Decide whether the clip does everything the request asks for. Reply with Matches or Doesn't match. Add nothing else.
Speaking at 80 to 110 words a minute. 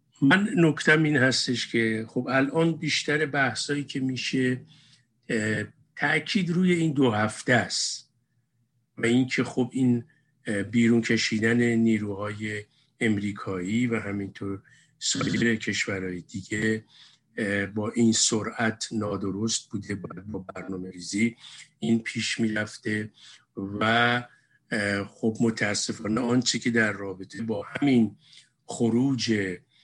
Matches